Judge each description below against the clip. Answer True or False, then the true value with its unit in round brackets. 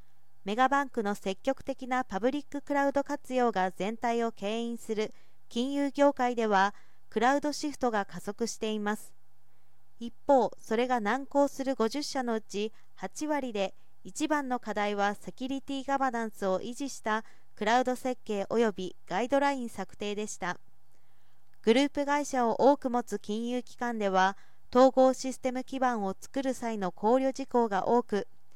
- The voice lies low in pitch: False (235 Hz)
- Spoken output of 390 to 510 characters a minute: False (305 characters per minute)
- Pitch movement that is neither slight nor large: True (4.6 semitones)